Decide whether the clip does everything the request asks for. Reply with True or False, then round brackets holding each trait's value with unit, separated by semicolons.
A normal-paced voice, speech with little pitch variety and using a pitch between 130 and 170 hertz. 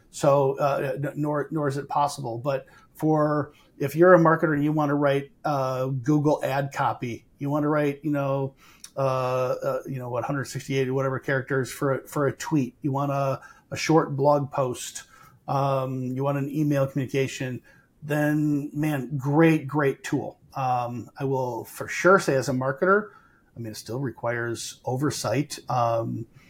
True (170 wpm; 2.1 semitones; 140 Hz)